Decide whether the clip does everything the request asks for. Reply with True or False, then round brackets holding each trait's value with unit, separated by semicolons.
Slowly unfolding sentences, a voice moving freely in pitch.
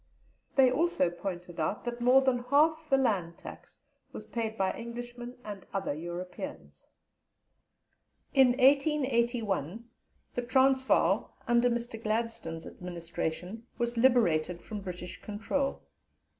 True (115 wpm; 5.7 semitones)